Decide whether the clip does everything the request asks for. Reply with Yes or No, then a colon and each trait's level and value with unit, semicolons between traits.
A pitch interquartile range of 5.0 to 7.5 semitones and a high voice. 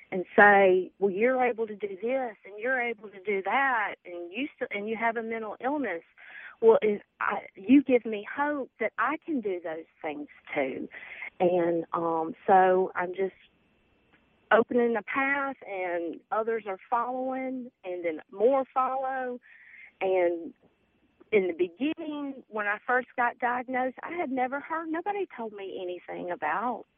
Yes: wide, 5.4 semitones; high, 230 Hz